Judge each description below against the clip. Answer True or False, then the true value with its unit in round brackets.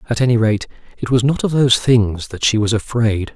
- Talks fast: True (230 wpm)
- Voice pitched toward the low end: True (115 Hz)